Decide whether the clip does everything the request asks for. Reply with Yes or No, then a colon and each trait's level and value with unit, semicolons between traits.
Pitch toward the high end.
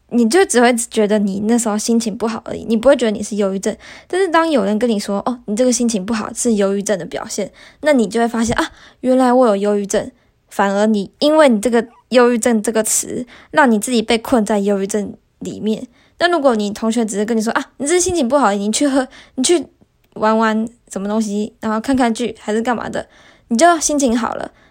Yes: high, 230 Hz